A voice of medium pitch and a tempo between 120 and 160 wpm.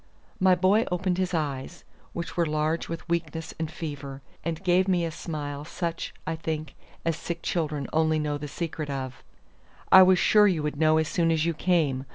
No: medium, 160 Hz; average, 195 wpm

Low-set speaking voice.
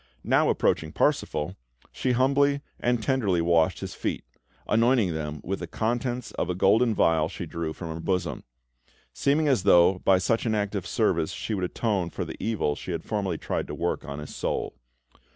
Yes: very low, 95 Hz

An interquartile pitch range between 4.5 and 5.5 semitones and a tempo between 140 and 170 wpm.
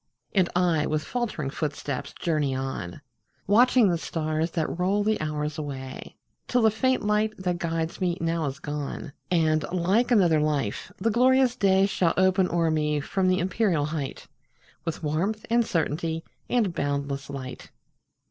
Yes: average, 4.8 semitones; average, 155 wpm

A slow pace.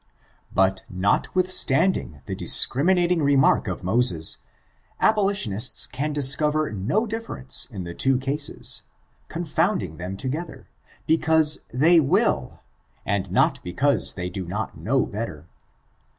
Yes: slow, 110 wpm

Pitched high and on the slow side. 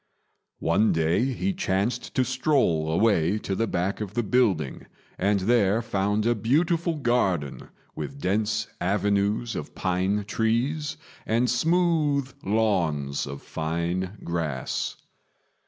No: low, 105 Hz; slow, 120 wpm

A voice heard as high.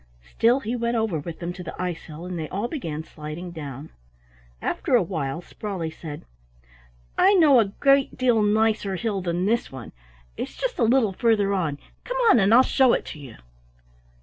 Yes: high, 195 Hz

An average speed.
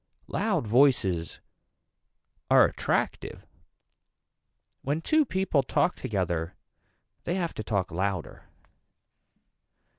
No: slow, 85 wpm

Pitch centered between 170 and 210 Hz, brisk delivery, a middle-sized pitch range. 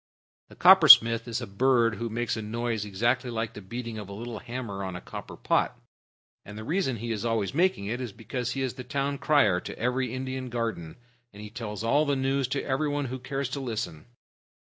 No: low, 120 Hz; fast, 210 wpm; average, 3.3 semitones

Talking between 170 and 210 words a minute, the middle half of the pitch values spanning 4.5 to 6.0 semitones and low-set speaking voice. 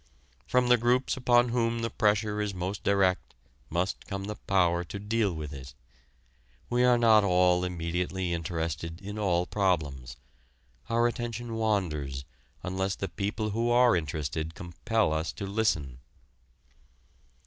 No: slow, 135 wpm; average, 5.0 semitones; very low, 95 Hz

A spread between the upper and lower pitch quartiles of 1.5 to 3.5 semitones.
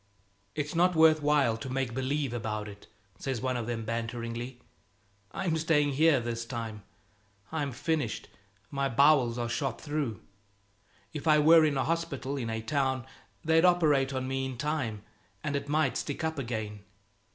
No: average, 4.5 semitones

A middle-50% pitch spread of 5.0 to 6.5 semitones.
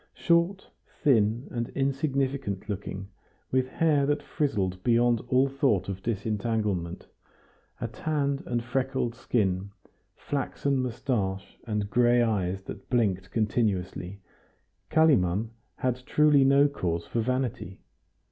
Yes: wide, 5.5 semitones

